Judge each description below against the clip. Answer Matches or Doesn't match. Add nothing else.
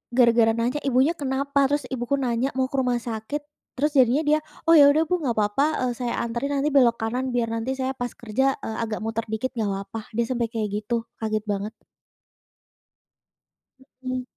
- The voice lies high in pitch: Matches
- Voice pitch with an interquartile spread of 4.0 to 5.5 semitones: Doesn't match